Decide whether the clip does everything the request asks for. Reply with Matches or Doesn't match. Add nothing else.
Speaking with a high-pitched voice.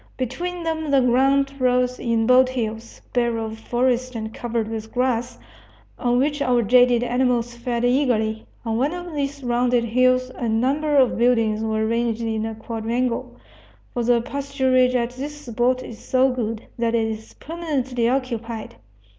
Matches